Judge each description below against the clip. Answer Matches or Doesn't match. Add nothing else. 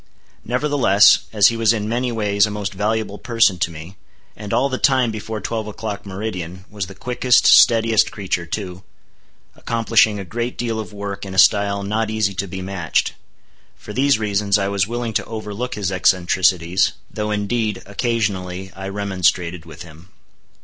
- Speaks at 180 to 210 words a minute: Doesn't match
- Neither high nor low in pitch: Doesn't match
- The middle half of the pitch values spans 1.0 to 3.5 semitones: Matches